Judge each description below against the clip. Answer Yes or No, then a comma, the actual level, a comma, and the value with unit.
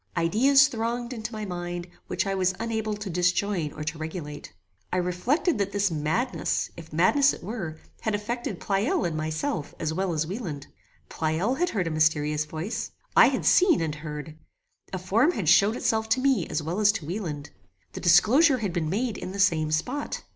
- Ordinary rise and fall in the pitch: No, wide, 6.0 semitones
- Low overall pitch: No, medium, 185 Hz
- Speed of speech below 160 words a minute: No, average, 190 wpm